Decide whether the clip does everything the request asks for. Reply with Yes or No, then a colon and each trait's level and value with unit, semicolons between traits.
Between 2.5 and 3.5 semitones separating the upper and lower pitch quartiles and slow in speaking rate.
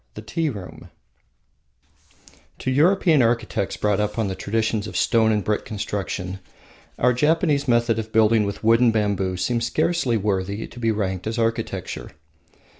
No: average, 2.8 semitones; average, 155 wpm